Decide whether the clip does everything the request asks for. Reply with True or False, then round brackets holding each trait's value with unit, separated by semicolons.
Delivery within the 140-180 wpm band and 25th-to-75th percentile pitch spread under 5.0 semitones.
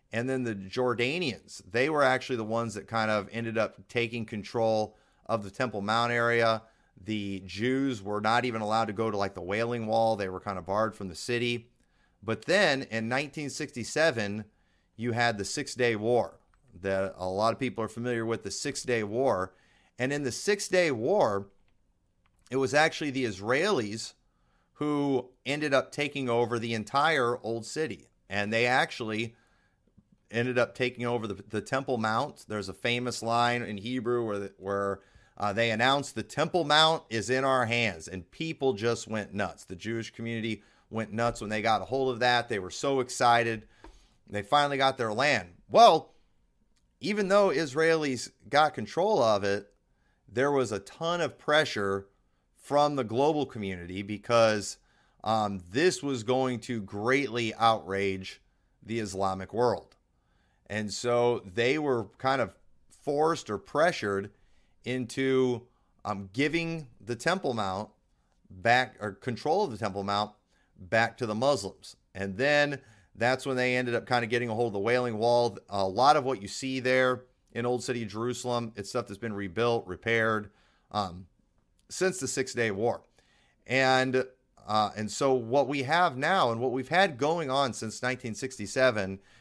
True (170 wpm; 3.9 semitones)